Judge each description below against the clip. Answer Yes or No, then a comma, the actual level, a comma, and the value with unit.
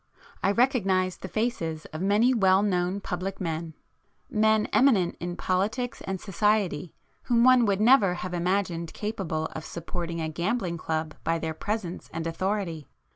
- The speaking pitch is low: No, medium, 185 Hz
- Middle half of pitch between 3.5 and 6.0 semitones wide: Yes, average, 4.1 semitones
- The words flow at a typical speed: Yes, average, 145 wpm